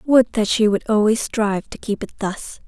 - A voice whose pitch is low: No, high, 215 Hz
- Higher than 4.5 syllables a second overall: Yes, 4.8 syllables/s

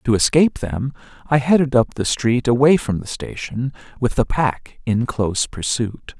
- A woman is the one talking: No, male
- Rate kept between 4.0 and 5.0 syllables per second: Yes, 4.7 syllables/s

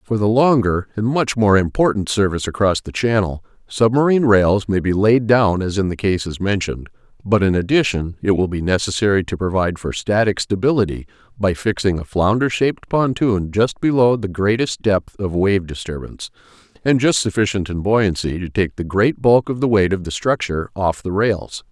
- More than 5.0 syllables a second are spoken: Yes, 5.3 syllables/s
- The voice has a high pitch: No, low, 100 Hz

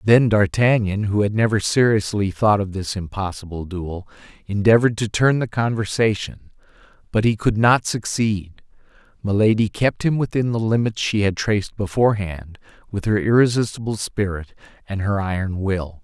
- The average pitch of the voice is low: Yes, low, 105 Hz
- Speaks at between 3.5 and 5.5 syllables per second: Yes, 5.0 syllables/s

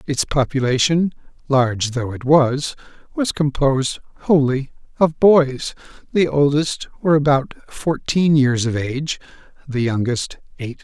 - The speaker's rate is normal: No, slow, 120 wpm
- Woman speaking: No, male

